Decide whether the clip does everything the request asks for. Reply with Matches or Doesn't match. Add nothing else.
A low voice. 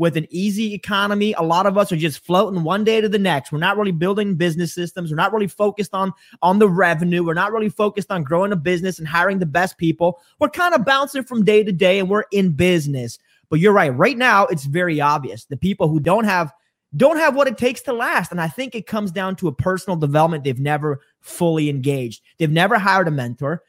Doesn't match